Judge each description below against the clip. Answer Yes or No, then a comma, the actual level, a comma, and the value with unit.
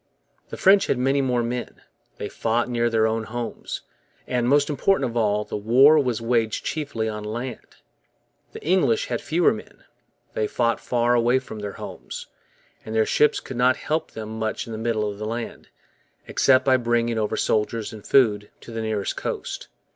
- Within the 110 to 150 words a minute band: No, average, 185 wpm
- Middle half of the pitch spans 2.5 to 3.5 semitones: Yes, average, 2.8 semitones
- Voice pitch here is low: Yes, low, 115 Hz